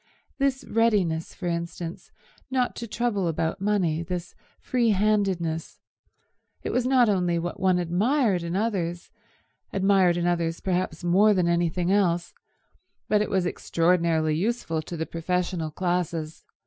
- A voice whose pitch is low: No, medium, 180 Hz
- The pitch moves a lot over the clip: No, average, 3.4 semitones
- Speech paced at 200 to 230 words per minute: No, slow, 135 wpm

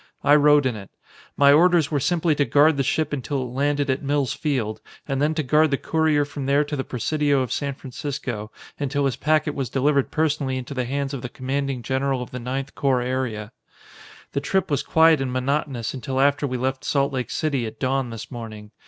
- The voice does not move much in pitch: Yes, narrow, 2.3 semitones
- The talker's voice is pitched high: No, medium, 140 Hz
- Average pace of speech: No, fast, 215 wpm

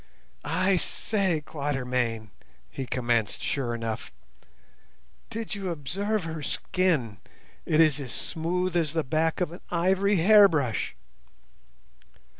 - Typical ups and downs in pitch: No, wide, 6.2 semitones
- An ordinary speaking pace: No, slow, 110 wpm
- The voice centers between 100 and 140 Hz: No, medium, 160 Hz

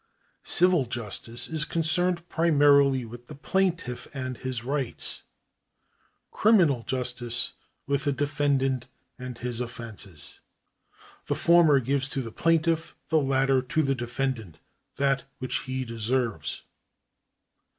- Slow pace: Yes, slow, 115 wpm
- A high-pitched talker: No, low, 135 Hz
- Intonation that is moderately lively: Yes, average, 3.8 semitones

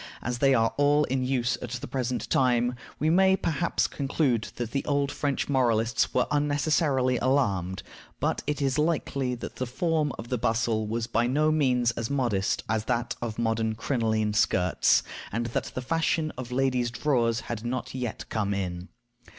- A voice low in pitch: Yes, low, 125 Hz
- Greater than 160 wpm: Yes, average, 175 wpm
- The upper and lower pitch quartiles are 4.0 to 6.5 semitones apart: No, average, 3.6 semitones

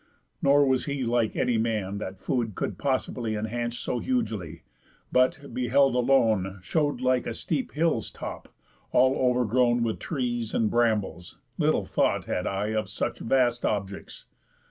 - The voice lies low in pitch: Yes, low, 120 Hz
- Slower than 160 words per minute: Yes, average, 145 wpm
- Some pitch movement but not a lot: Yes, average, 3.3 semitones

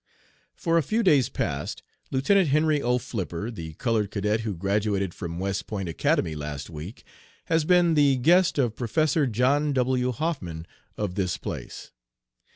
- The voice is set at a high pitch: No, low, 120 Hz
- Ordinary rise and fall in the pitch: No, wide, 7.4 semitones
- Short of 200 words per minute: Yes, average, 155 wpm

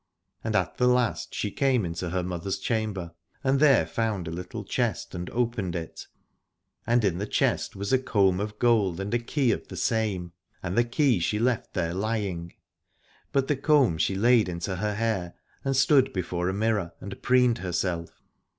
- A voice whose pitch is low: Yes, low, 105 Hz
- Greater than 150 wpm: Yes, average, 185 wpm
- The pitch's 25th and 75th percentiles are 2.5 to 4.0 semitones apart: No, average, 5.0 semitones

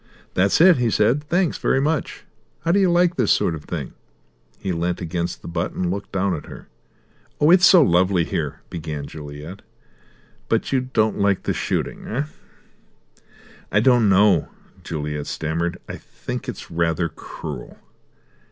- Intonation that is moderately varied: No, wide, 8.1 semitones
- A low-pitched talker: Yes, very low, 95 Hz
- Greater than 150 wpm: Yes, average, 160 wpm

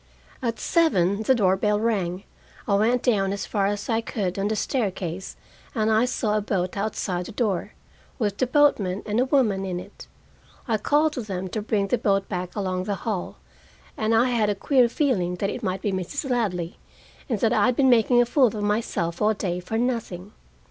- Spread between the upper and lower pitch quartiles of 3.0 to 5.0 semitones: Yes, average, 3.7 semitones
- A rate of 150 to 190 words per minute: No, fast, 205 wpm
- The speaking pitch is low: No, high, 210 Hz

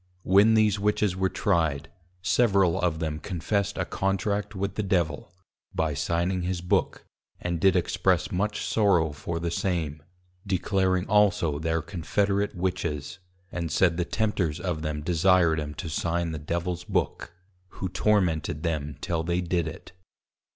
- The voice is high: No, very low, 90 Hz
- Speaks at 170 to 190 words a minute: No, average, 150 wpm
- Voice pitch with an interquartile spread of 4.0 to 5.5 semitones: No, average, 3.2 semitones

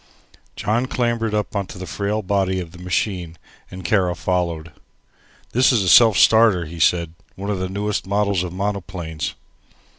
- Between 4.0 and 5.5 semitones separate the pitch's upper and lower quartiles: No, average, 3.0 semitones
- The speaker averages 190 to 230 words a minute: No, average, 160 wpm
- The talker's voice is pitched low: Yes, very low, 95 Hz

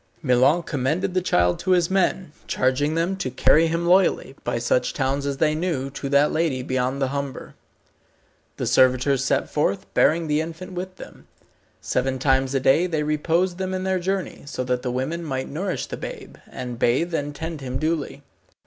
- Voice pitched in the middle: Yes, medium, 150 Hz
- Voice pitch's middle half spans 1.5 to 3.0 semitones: No, average, 4.5 semitones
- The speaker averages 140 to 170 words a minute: No, average, 185 wpm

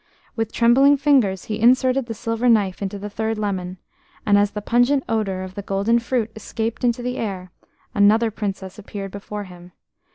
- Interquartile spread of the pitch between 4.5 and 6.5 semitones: No, average, 3.1 semitones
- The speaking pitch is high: Yes, high, 215 Hz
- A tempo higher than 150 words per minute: Yes, average, 175 wpm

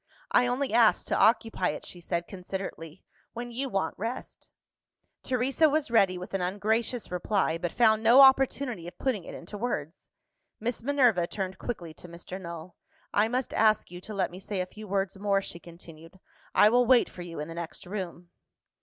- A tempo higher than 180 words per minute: Yes, average, 190 wpm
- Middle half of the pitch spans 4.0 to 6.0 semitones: Yes, average, 5.2 semitones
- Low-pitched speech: No, high, 195 Hz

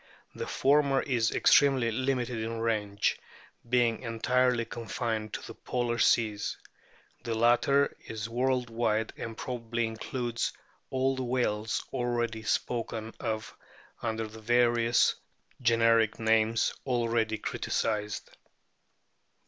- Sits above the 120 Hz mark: No, low, 115 Hz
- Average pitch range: No, narrow, 1.6 semitones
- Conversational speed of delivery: No, slow, 110 wpm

